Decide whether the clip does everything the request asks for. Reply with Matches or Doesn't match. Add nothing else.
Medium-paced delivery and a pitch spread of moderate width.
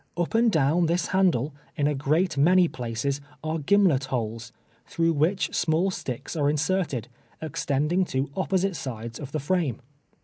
Matches